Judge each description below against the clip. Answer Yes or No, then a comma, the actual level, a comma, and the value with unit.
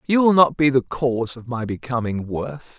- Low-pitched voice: Yes, low, 130 Hz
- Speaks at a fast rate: Yes, fast, 215 wpm